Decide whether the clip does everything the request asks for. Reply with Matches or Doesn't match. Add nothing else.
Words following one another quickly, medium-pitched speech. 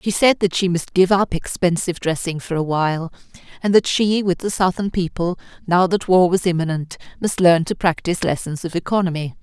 Doesn't match